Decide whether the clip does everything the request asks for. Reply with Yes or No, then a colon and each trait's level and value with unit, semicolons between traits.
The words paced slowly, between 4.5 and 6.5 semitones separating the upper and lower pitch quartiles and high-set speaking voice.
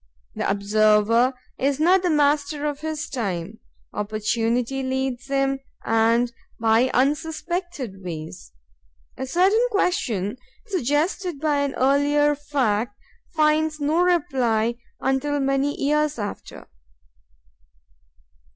Yes: slow, 95 wpm; average, 4.8 semitones; very high, 275 Hz